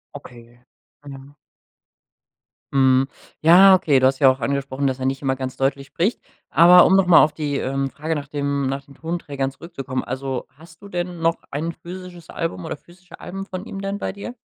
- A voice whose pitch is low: No, medium, 145 Hz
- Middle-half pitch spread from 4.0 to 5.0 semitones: Yes, average, 4.5 semitones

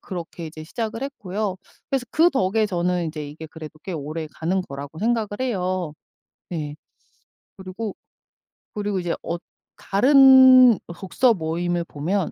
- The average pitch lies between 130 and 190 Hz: Yes, medium, 185 Hz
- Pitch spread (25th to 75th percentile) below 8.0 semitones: Yes, average, 5.3 semitones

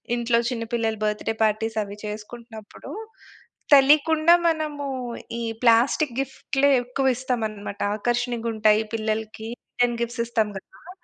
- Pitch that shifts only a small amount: No, average, 3.2 semitones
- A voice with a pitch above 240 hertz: No, high, 235 Hz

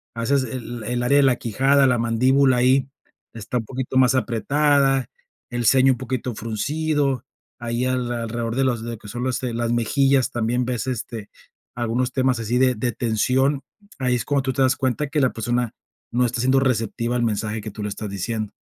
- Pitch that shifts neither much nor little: No, narrow, 2.2 semitones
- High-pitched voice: No, low, 125 Hz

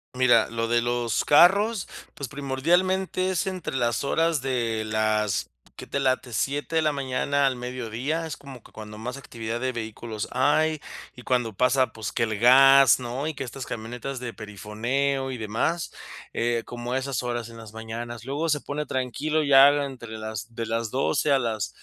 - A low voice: Yes, low, 125 Hz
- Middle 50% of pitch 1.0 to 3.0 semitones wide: No, average, 3.5 semitones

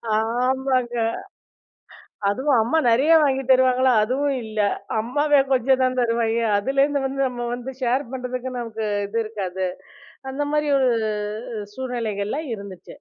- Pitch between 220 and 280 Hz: Yes, very high, 255 Hz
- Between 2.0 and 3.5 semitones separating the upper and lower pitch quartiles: Yes, average, 2.8 semitones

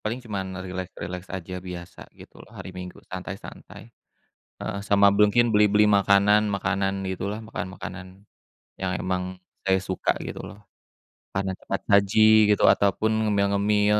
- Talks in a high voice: No, low, 100 Hz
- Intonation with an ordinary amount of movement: No, narrow, 1.9 semitones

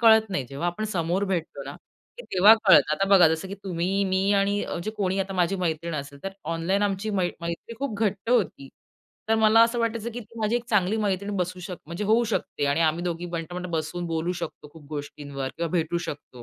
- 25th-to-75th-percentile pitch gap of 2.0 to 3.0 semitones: No, average, 3.7 semitones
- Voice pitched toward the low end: No, medium, 185 Hz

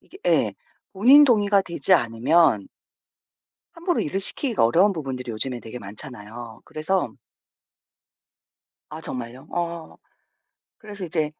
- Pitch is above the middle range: No, medium, 155 Hz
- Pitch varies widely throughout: Yes, wide, 8.2 semitones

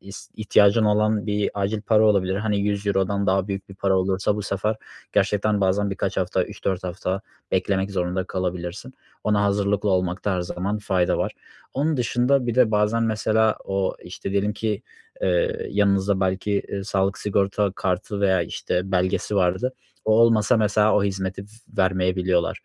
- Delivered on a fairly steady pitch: Yes, narrow, 2.0 semitones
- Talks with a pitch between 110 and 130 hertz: No, low, 100 Hz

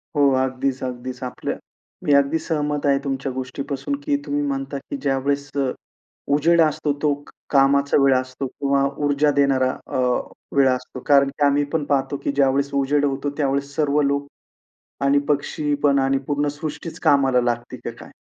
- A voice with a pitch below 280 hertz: Yes, medium, 140 Hz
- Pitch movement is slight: Yes, narrow, 1.2 semitones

